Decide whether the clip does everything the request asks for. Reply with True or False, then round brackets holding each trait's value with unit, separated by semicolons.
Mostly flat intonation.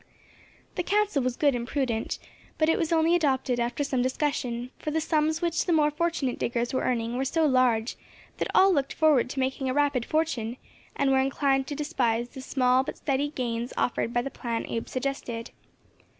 False (3.7 semitones)